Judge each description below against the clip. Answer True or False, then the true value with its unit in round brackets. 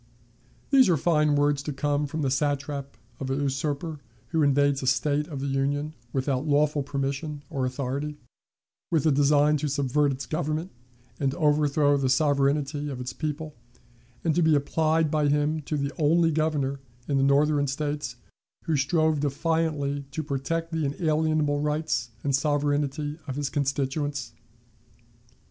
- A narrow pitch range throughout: True (1.7 semitones)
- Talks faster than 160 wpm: False (155 wpm)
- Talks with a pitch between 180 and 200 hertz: False (145 Hz)